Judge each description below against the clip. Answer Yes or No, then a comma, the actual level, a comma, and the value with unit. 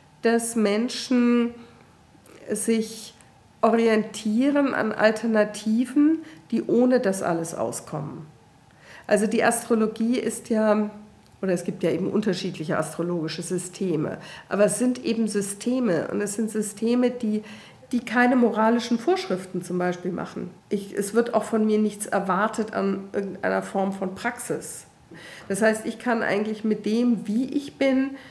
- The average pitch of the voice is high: Yes, high, 215 Hz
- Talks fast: No, average, 135 wpm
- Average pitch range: Yes, average, 3.3 semitones